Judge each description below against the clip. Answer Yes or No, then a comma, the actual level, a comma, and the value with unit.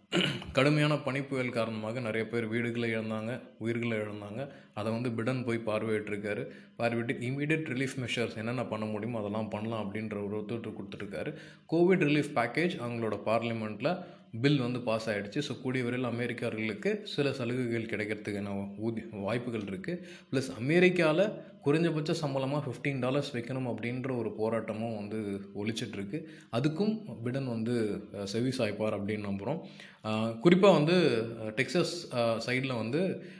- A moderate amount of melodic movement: Yes, average, 4.3 semitones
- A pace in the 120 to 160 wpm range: Yes, average, 125 wpm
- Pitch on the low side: Yes, low, 120 Hz